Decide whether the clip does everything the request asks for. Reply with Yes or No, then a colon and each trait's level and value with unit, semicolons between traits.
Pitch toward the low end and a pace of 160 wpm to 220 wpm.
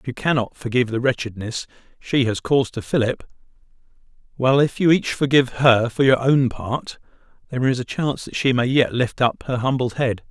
Yes: low, 125 Hz; average, 200 wpm